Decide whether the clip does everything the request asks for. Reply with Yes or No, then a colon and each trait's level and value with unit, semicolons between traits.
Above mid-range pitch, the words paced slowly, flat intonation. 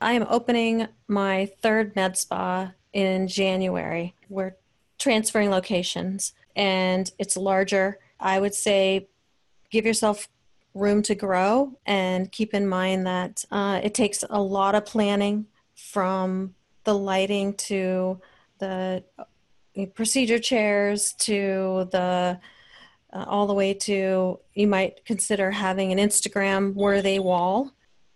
Yes: high, 195 Hz; slow, 120 wpm; narrow, 1.7 semitones